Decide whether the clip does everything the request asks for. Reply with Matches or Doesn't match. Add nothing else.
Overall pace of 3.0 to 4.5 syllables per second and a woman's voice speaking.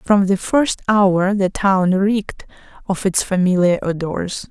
Matches